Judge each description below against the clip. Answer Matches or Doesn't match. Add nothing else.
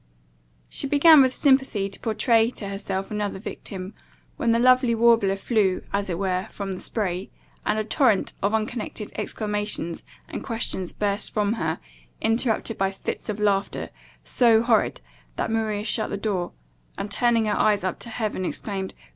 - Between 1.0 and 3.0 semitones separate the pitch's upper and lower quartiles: Matches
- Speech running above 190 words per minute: Doesn't match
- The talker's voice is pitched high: Matches